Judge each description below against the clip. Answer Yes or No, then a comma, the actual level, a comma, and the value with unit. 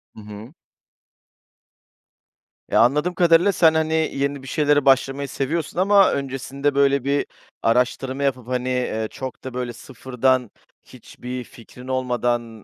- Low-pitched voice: Yes, low, 130 Hz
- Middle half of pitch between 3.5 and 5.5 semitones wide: No, narrow, 2.4 semitones